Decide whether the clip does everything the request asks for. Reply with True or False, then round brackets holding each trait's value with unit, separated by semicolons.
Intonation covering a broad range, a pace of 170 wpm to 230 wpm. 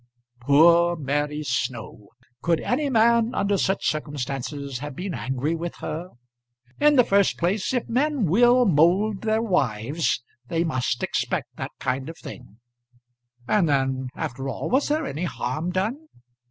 False (7.7 semitones; 145 wpm)